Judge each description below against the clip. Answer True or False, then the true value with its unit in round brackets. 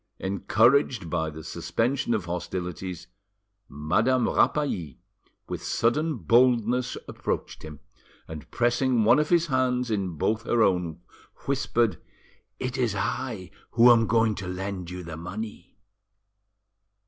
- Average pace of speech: False (125 wpm)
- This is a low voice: True (110 Hz)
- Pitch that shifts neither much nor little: False (5.8 semitones)